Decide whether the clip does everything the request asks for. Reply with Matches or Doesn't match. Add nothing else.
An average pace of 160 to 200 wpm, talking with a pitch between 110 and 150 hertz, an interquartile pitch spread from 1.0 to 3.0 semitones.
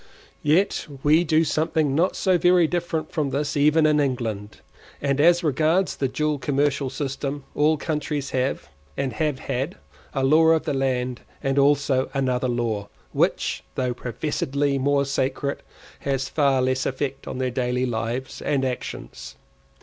Doesn't match